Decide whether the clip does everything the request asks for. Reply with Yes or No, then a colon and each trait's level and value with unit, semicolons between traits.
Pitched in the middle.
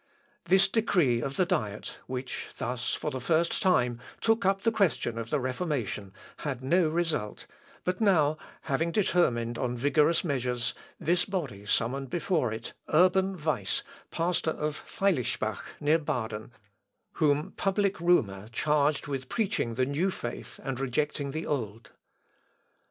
Yes: medium, 150 Hz